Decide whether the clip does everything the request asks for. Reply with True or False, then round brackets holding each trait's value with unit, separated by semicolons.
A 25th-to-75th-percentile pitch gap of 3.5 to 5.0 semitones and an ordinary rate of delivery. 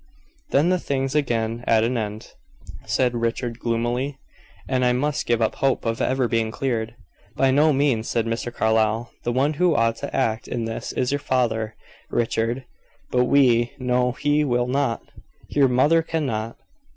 False (3.0 semitones; 165 wpm)